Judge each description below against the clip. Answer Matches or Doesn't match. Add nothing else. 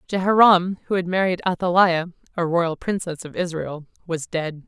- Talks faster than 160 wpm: Doesn't match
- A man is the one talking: Doesn't match